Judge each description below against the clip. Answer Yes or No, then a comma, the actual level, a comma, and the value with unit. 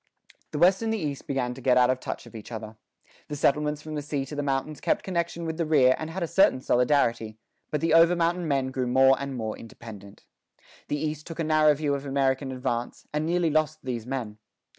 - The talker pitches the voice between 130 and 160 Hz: Yes, medium, 140 Hz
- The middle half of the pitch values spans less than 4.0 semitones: Yes, average, 3.5 semitones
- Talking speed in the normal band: No, fast, 225 wpm